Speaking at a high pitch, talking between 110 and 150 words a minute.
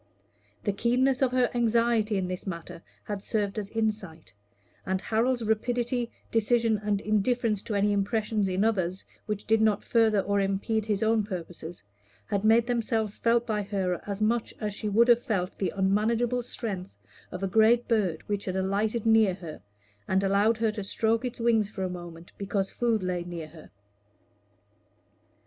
No: high, 210 Hz; average, 170 wpm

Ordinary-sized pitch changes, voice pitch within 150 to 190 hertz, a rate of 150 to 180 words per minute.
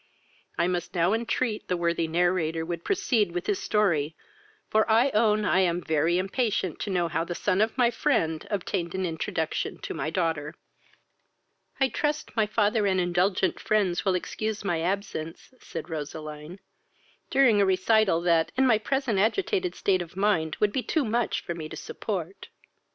Yes: average, 4.3 semitones; medium, 185 Hz; average, 170 wpm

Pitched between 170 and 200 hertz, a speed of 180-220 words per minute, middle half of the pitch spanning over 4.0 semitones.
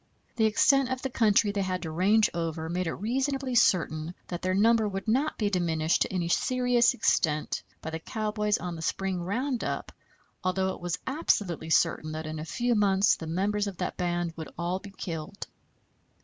Yes: high, 190 Hz; average, 190 wpm; average, 4.5 semitones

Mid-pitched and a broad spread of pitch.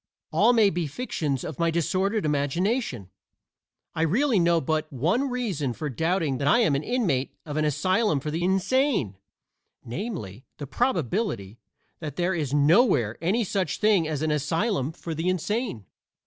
Yes: medium, 165 Hz; wide, 6.3 semitones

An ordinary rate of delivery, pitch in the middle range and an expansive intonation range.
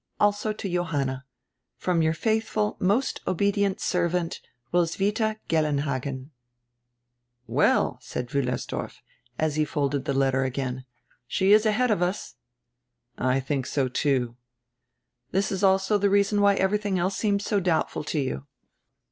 No: slow, 130 wpm; medium, 175 Hz; wide, 6.5 semitones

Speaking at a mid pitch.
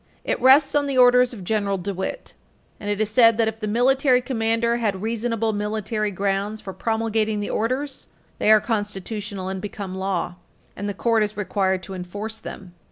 No: high, 215 Hz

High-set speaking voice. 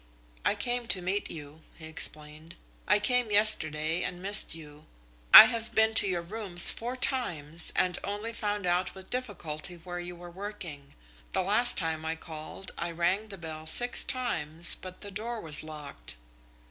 No: medium, 180 Hz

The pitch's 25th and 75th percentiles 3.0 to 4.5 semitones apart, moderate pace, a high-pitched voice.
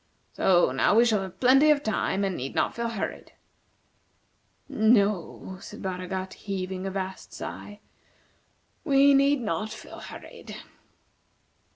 No: average, 3.9 semitones; slow, 130 wpm; high, 200 Hz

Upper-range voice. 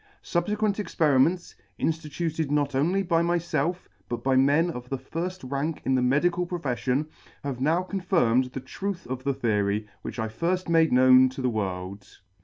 No: medium, 145 Hz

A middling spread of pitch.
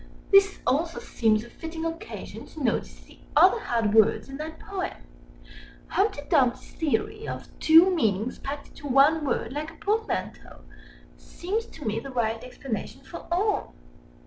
No: wide, 6.6 semitones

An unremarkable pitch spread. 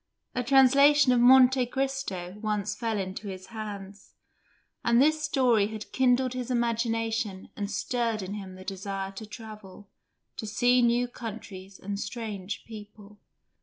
Yes: average, 3.6 semitones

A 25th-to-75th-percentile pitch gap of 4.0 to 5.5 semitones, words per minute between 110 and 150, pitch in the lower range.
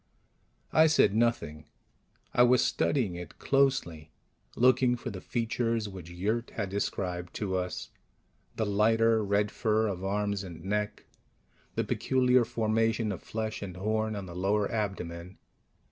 No: average, 3.4 semitones; average, 140 wpm; low, 105 Hz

